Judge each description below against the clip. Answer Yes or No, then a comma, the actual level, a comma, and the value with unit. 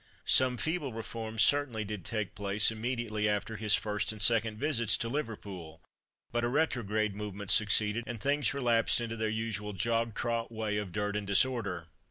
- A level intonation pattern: Yes, narrow, 2.2 semitones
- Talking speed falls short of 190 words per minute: Yes, average, 170 wpm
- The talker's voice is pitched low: Yes, low, 110 Hz